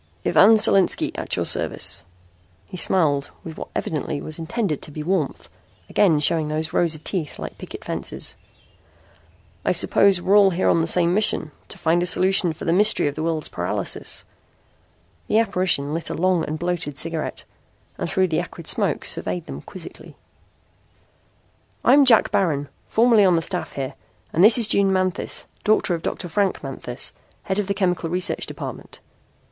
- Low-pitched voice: No, medium, 175 Hz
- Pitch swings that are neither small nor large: Yes, average, 3.8 semitones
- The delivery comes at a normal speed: Yes, average, 170 wpm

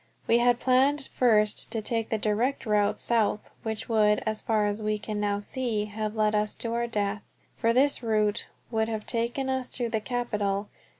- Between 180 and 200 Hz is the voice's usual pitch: No, high, 220 Hz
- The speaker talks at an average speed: Yes, average, 190 wpm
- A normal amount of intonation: No, narrow, 2.2 semitones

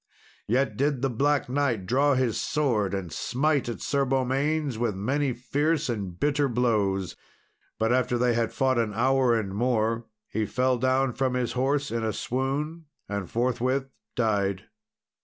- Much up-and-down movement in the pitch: No, average, 3.3 semitones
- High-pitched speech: No, low, 125 Hz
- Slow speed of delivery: No, average, 160 wpm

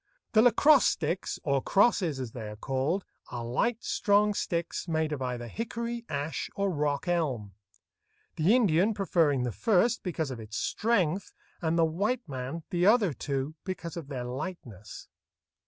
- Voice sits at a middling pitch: Yes, medium, 165 Hz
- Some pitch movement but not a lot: No, wide, 7.1 semitones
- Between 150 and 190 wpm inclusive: Yes, average, 155 wpm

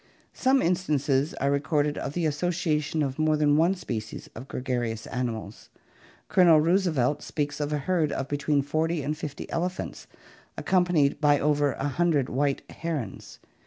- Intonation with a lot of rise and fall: No, average, 3.0 semitones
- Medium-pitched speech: Yes, medium, 150 Hz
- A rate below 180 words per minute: Yes, average, 150 wpm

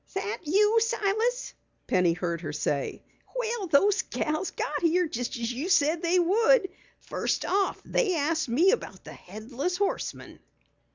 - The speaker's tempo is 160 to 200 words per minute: No, average, 150 wpm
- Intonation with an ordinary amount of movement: No, wide, 8.5 semitones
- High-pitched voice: Yes, very high, 350 Hz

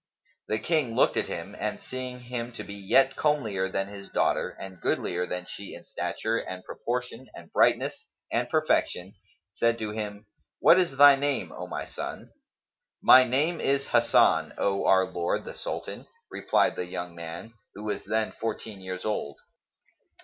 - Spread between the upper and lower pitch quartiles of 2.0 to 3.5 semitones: No, average, 4.9 semitones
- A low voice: Yes, low, 110 Hz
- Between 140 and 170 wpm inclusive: Yes, average, 165 wpm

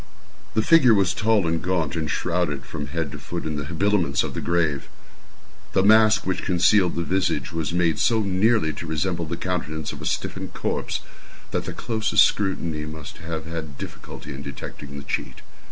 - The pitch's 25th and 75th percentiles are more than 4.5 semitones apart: No, average, 3.8 semitones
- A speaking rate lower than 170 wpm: No, average, 185 wpm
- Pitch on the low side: Yes, very low, 85 Hz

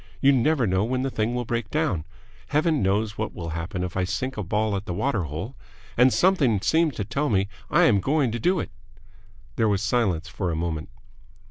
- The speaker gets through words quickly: Yes, fast, 220 wpm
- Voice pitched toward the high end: No, low, 110 Hz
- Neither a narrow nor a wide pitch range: No, wide, 5.9 semitones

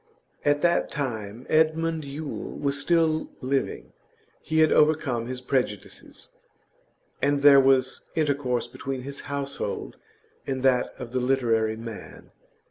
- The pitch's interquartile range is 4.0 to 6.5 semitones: No, average, 2.8 semitones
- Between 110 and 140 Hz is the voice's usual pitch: Yes, low, 135 Hz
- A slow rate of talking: Yes, slow, 125 wpm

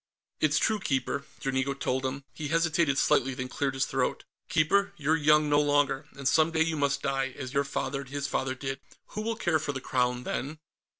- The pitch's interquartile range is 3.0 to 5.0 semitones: No, narrow, 2.6 semitones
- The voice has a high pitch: No, medium, 140 Hz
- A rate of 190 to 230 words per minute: Yes, fast, 205 wpm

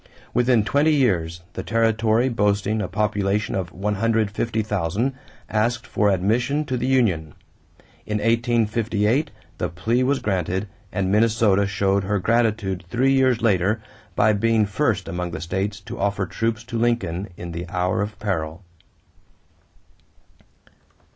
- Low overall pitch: Yes, low, 105 Hz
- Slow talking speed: Yes, slow, 130 wpm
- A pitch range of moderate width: Yes, average, 3.2 semitones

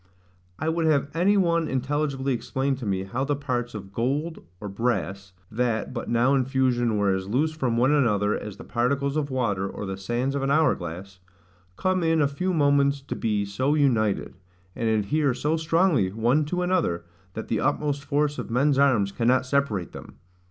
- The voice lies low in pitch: Yes, low, 130 Hz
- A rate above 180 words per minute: Yes, average, 190 wpm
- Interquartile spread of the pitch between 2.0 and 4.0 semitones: No, average, 5.0 semitones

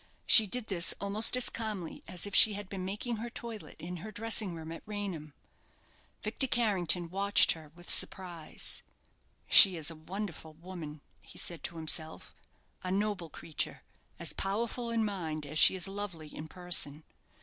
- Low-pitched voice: No, medium, 185 Hz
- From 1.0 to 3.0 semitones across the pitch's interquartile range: No, average, 4.3 semitones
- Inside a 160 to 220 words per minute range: Yes, average, 165 wpm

